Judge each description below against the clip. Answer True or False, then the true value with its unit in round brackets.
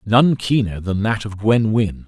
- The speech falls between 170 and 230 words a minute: True (200 wpm)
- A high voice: False (110 Hz)